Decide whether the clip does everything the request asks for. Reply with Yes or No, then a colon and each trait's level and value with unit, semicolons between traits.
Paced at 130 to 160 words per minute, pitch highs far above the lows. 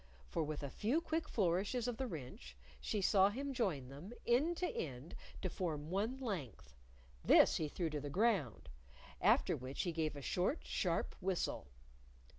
No: average, 170 wpm; wide, 8.1 semitones